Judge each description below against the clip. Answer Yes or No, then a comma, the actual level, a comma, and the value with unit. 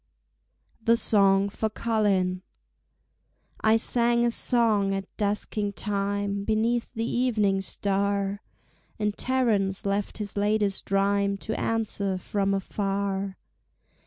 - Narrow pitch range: Yes, narrow, 1.9 semitones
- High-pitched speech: Yes, high, 200 Hz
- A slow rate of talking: Yes, slow, 105 wpm